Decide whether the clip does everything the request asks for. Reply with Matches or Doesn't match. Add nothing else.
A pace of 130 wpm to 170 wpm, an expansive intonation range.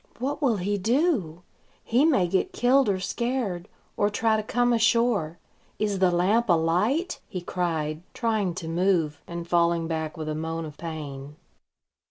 Matches